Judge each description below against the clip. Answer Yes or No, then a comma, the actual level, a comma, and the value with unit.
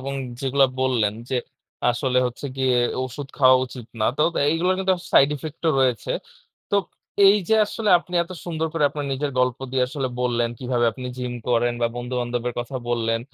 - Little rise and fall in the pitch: No, average, 3.4 semitones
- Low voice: Yes, low, 130 Hz